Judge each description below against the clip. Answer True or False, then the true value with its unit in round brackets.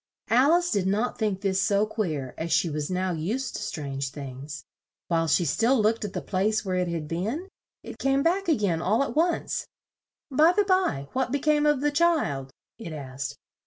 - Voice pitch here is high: True (200 Hz)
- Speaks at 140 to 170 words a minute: False (200 wpm)